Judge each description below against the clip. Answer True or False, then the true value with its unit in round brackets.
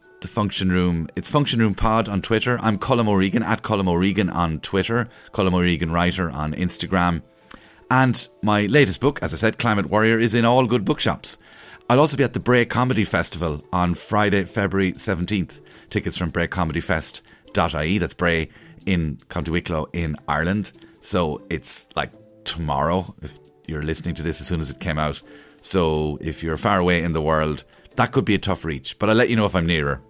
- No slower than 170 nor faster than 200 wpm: True (190 wpm)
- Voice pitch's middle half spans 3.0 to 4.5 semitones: False (5.1 semitones)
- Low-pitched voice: True (90 Hz)